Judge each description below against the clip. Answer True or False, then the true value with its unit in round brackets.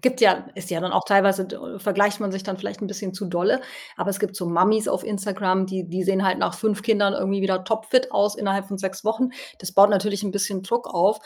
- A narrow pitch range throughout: True (1.6 semitones)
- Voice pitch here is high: True (195 Hz)